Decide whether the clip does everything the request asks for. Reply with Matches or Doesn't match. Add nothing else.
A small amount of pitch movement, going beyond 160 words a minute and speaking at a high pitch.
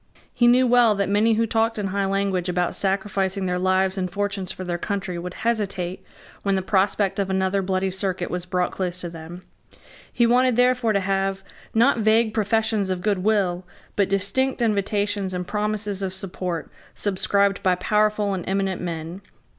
Matches